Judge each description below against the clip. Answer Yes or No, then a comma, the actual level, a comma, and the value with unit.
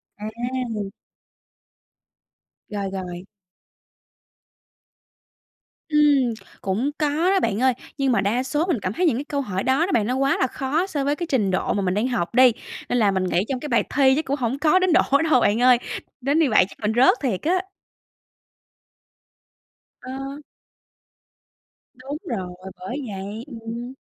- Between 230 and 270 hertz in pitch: Yes, very high, 255 Hz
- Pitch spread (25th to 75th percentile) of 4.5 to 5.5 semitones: Yes, average, 5.2 semitones